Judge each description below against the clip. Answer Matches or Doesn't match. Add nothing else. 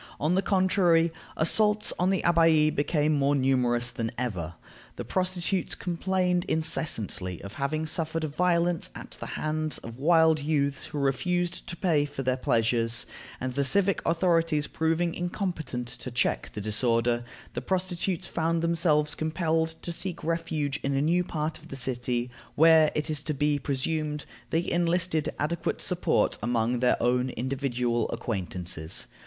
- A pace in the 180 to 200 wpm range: Doesn't match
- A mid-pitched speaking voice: Matches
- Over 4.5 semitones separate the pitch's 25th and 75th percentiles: Matches